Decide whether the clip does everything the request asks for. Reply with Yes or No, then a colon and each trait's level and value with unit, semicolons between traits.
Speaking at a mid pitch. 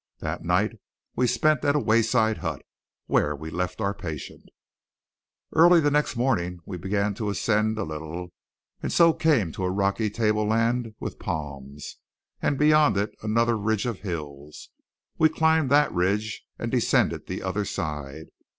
No: low, 105 Hz